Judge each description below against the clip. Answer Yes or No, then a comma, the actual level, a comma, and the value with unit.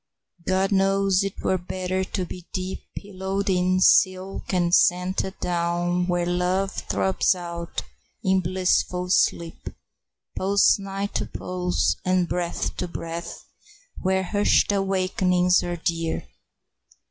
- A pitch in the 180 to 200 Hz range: Yes, medium, 185 Hz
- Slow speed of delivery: Yes, slow, 115 wpm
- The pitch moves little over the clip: Yes, narrow, 1.3 semitones